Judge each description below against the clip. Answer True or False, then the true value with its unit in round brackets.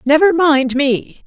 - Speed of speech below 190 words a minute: True (140 wpm)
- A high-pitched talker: True (290 Hz)